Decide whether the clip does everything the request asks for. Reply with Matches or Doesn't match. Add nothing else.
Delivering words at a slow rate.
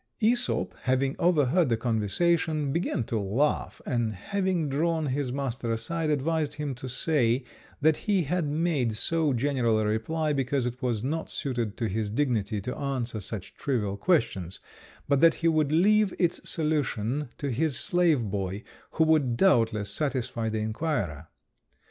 Doesn't match